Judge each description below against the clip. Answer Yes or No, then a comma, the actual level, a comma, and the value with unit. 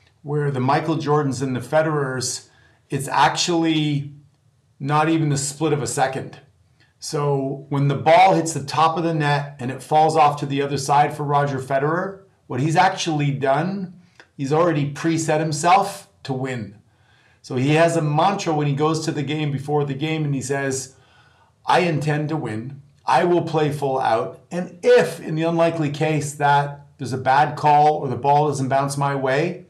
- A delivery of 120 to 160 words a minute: No, average, 185 wpm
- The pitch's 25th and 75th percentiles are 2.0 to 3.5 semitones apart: Yes, average, 2.7 semitones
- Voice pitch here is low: No, medium, 145 Hz